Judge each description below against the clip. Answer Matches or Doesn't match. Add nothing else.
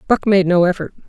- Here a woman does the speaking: Matches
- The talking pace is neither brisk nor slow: Doesn't match